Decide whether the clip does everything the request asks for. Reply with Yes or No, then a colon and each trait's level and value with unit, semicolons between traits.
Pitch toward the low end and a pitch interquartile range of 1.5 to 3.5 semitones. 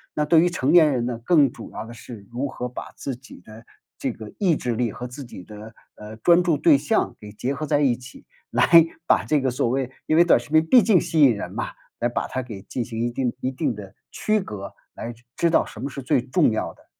No: low, 125 Hz; average, 4.5 semitones